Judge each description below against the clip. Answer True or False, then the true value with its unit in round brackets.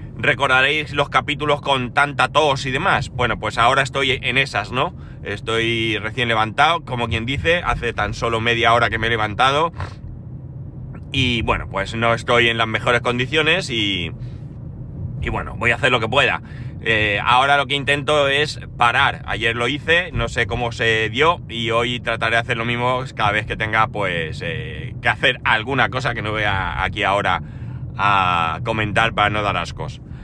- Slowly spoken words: False (185 wpm)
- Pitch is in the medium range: False (120 Hz)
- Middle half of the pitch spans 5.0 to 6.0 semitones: False (3.1 semitones)